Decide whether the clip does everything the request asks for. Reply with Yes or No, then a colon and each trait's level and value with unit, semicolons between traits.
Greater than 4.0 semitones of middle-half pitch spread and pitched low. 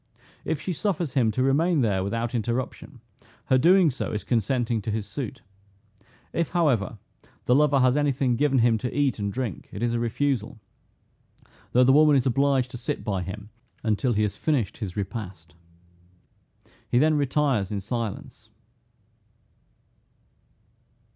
Yes: average, 4.6 semitones; low, 125 Hz